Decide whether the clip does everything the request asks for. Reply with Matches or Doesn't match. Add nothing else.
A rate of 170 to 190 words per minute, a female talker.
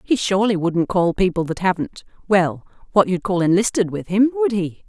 Matches